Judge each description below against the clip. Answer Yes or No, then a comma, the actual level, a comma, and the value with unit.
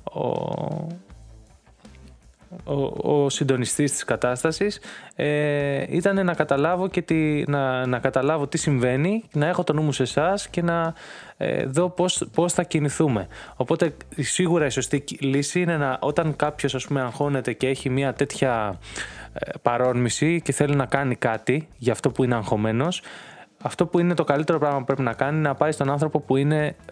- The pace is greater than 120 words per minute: Yes, fast, 170 wpm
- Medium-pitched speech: Yes, medium, 145 Hz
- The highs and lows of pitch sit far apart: No, average, 4.1 semitones